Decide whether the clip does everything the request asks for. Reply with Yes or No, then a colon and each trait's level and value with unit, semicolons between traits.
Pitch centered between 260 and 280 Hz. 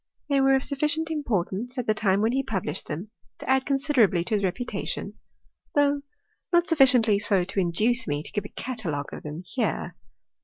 No: high, 225 Hz